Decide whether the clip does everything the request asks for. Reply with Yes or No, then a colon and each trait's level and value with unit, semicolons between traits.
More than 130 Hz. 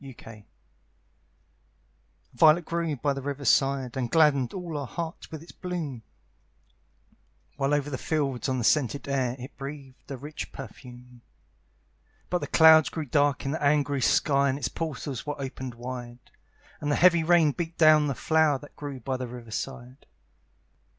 Yes: medium, 140 Hz